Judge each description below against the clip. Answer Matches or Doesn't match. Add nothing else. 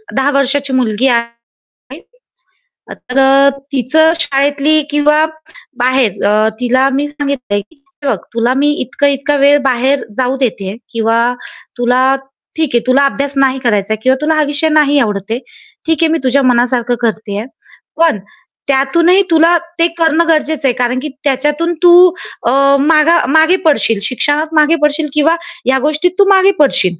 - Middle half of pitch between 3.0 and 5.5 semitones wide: Matches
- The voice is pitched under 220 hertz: Doesn't match